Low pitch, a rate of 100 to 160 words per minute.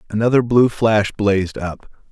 Yes: low, 105 Hz; average, 140 wpm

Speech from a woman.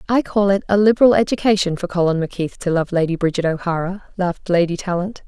Yes: female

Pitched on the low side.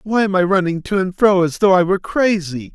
No: medium, 185 Hz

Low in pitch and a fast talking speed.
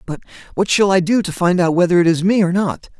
No: medium, 180 Hz; fast, 280 wpm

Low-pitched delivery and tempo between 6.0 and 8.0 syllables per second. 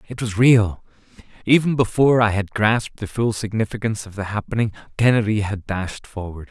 No: low, 110 Hz; 5.6 syllables/s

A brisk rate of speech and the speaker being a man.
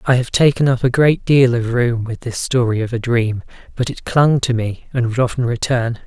Yes: fast, 235 wpm; male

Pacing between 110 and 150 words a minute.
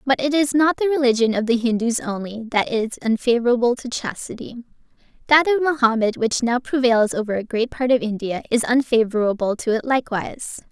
No: average, 180 wpm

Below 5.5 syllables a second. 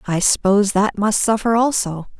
Yes: 5.1 syllables/s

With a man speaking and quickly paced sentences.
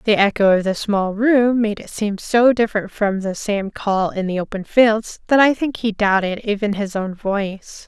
No: female; fast, 215 wpm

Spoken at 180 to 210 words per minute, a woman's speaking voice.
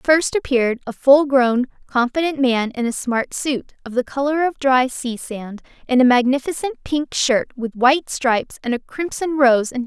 Yes: average, 200 wpm; female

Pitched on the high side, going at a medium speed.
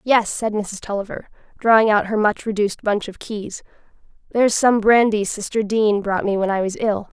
Yes: high, 210 Hz; average, 190 wpm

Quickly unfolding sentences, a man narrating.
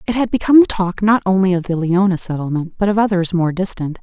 No: fast, 240 wpm; female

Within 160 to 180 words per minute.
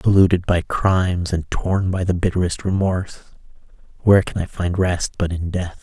Yes: average, 175 wpm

